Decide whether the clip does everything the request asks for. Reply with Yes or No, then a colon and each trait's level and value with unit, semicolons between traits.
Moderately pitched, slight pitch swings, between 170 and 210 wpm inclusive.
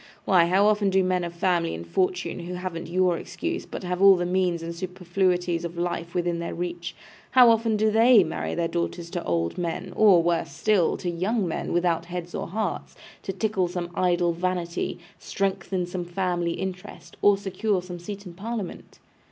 Yes: medium, 180 Hz; narrow, 2.0 semitones; average, 185 wpm